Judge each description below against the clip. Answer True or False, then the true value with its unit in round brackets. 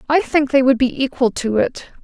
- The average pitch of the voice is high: True (265 Hz)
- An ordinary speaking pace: False (235 wpm)